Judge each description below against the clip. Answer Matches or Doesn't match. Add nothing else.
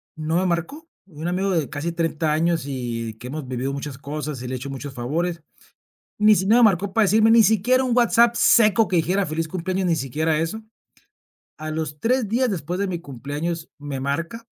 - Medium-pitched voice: Matches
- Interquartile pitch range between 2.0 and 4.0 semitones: Doesn't match